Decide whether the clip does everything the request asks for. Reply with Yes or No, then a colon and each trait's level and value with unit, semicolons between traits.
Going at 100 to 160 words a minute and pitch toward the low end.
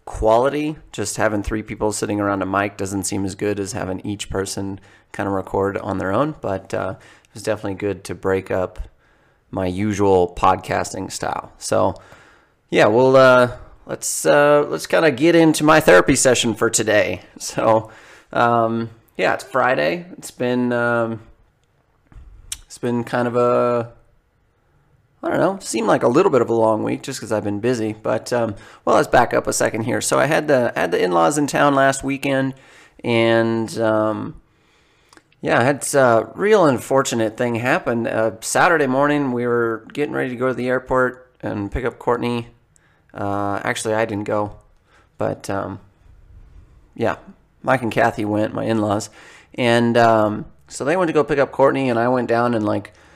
No: average, 175 wpm; low, 115 Hz